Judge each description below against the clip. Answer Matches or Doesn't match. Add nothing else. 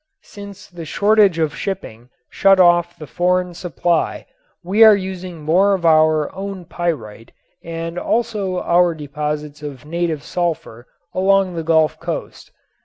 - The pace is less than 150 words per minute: Matches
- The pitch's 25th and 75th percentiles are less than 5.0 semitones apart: Matches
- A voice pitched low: Doesn't match